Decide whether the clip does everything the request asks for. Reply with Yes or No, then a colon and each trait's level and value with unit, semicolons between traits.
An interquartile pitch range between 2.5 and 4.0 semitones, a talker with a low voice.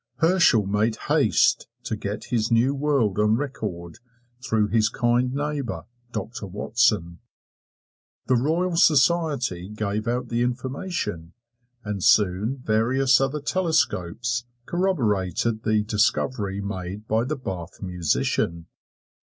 No: average, 4.7 semitones; low, 115 Hz